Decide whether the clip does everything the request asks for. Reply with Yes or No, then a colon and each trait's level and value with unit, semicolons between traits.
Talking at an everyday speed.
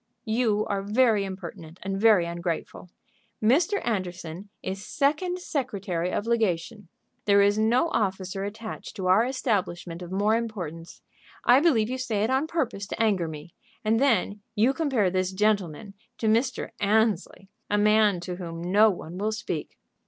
Yes: average, 155 wpm